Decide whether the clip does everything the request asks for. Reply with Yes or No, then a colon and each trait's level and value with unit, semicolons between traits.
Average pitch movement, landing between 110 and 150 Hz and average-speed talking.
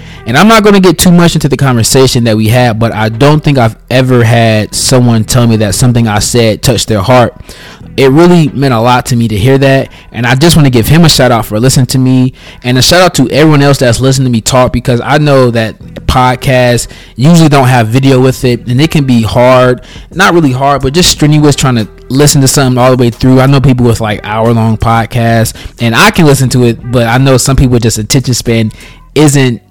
No: average, 3.1 semitones; low, 125 Hz; fast, 245 wpm